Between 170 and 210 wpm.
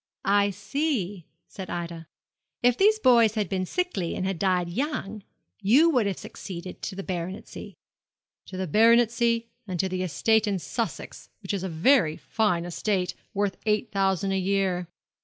No: average, 160 wpm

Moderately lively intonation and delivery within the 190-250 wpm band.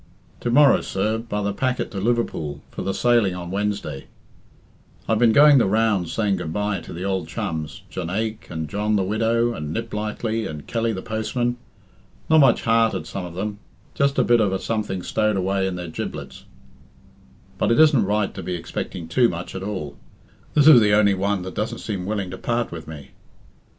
Yes: average, 3.6 semitones; average, 195 wpm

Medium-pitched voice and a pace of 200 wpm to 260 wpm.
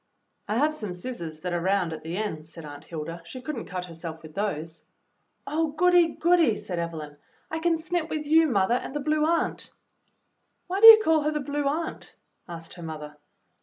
No: high, 215 Hz; fast, 205 wpm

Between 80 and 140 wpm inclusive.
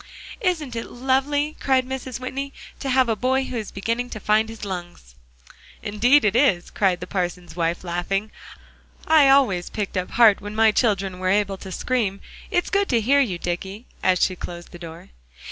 No: average, 185 wpm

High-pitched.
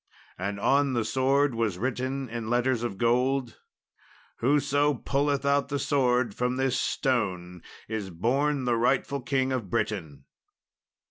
No: low, 125 Hz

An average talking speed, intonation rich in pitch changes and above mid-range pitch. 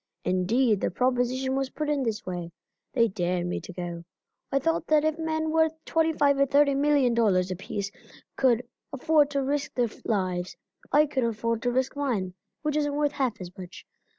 Yes: average, 185 wpm; wide, 6.5 semitones; very high, 260 Hz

